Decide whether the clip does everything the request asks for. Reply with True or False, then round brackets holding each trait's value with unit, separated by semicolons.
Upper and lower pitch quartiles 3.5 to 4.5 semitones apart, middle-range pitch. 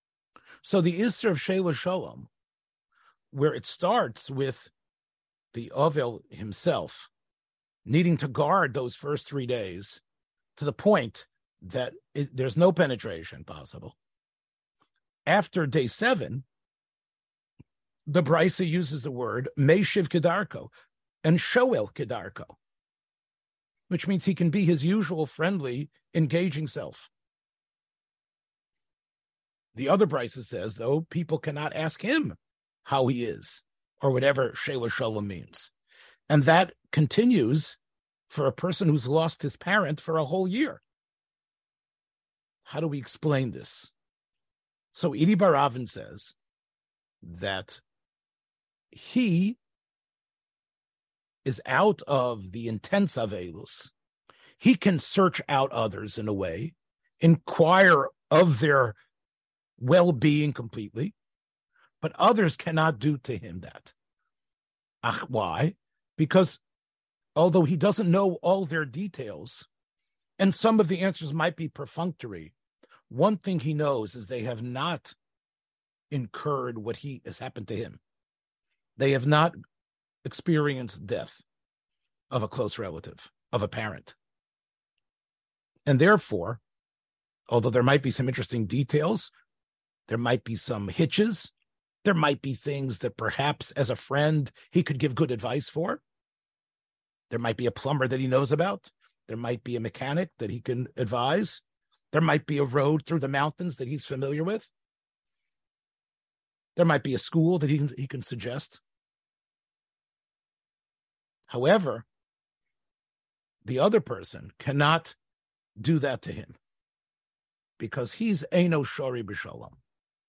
False (5.2 semitones; 150 Hz)